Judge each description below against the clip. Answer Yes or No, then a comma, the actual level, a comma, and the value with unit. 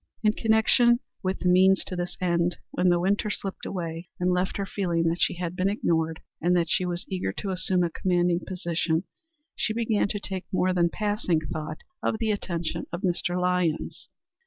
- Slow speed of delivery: No, average, 190 wpm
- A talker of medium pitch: Yes, medium, 180 Hz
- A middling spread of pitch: No, narrow, 2.1 semitones